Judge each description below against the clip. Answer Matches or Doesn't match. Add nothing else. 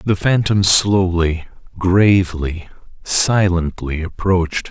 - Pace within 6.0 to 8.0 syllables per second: Doesn't match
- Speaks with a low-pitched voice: Matches